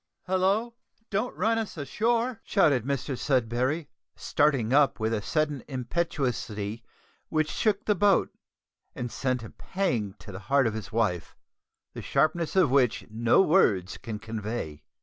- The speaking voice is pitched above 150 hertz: No, low, 135 Hz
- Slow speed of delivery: No, average, 145 wpm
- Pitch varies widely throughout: Yes, wide, 8.3 semitones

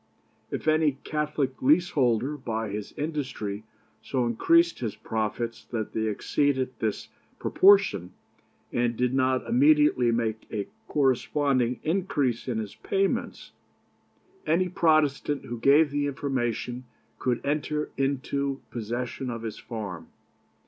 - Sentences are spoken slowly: Yes, slow, 115 wpm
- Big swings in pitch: No, average, 4.4 semitones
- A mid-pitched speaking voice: No, low, 130 Hz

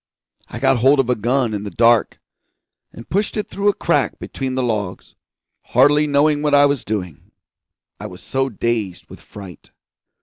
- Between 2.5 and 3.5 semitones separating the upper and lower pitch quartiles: No, average, 5.1 semitones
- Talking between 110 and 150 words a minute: No, average, 175 wpm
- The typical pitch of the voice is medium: No, low, 125 Hz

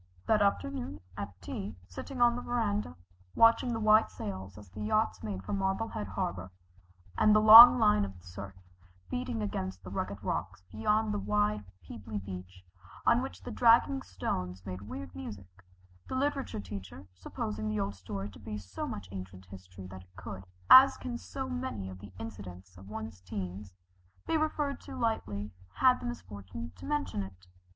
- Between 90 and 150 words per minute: No, average, 170 wpm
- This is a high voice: No, low, 100 Hz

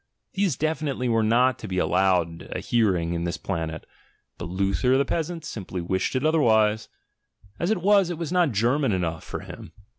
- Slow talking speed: No, average, 180 wpm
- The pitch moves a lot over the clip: Yes, wide, 8.8 semitones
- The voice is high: No, low, 115 Hz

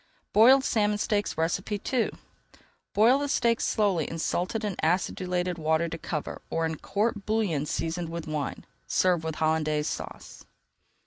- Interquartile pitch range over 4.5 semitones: Yes, average, 4.9 semitones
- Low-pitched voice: No, medium, 180 Hz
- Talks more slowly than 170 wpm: Yes, average, 140 wpm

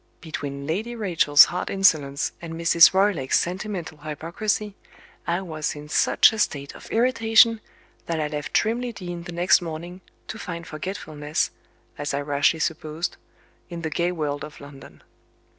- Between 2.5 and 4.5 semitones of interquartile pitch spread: Yes, average, 4.2 semitones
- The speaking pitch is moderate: Yes, medium, 170 Hz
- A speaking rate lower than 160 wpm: Yes, average, 150 wpm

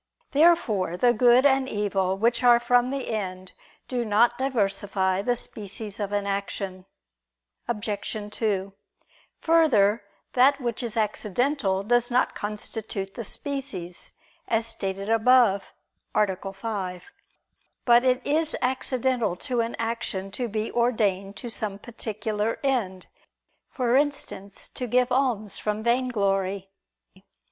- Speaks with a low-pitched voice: No, high, 220 Hz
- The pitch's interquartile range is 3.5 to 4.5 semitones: Yes, average, 3.8 semitones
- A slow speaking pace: Yes, slow, 120 wpm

